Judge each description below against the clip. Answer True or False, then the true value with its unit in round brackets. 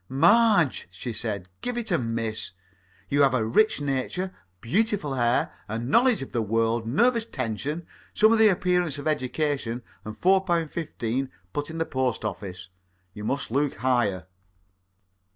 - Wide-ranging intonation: True (7.6 semitones)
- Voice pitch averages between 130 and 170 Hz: True (135 Hz)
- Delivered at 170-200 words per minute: False (160 wpm)